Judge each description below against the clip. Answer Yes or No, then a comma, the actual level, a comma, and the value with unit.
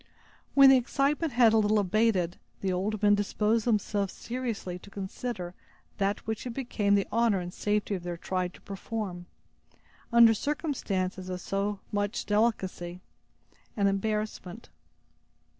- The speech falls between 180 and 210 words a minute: No, average, 140 wpm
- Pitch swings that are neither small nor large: Yes, average, 3.4 semitones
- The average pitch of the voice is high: Yes, high, 205 Hz